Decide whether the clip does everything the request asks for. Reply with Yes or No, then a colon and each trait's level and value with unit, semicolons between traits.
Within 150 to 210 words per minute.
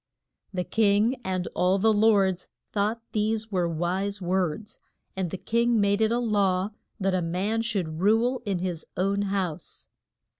Yes: average, 155 wpm